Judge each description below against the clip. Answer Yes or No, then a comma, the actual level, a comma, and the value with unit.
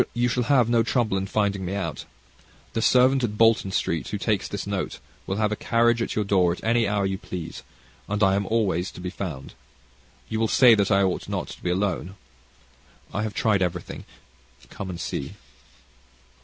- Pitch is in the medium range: No, low, 100 Hz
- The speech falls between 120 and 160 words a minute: No, average, 195 wpm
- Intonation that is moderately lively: Yes, average, 3.2 semitones